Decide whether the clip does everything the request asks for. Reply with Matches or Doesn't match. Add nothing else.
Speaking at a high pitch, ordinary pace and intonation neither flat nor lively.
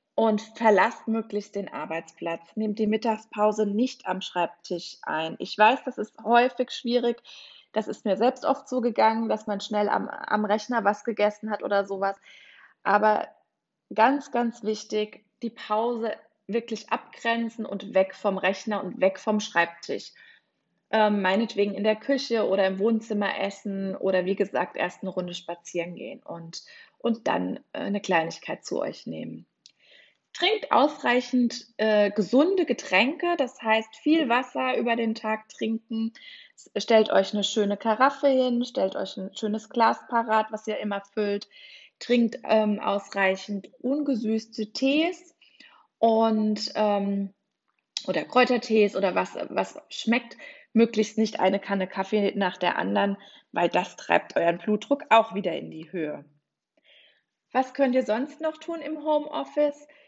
Matches